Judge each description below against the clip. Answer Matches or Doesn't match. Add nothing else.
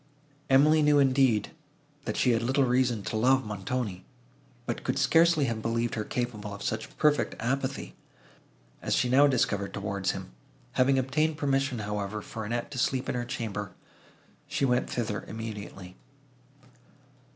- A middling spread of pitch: Matches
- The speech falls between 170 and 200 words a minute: Doesn't match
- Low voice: Matches